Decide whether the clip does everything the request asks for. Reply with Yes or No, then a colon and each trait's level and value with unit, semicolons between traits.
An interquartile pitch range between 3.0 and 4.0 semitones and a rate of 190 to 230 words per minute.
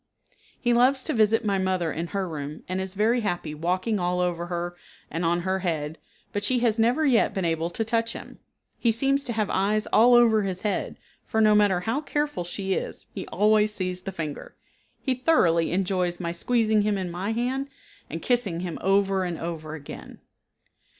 No: average, 4.4 semitones; average, 195 wpm